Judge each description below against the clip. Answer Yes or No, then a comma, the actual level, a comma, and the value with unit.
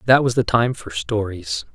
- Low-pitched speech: Yes, low, 105 Hz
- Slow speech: No, fast, 205 wpm